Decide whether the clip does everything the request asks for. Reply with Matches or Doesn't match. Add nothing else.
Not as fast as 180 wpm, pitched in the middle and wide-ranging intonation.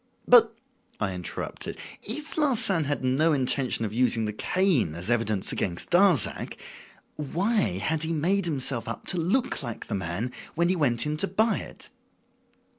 Matches